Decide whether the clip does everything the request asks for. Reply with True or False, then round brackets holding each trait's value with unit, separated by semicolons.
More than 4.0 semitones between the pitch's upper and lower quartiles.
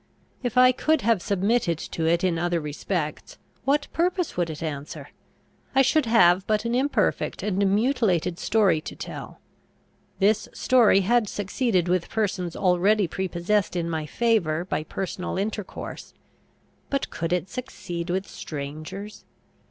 True (5.0 semitones)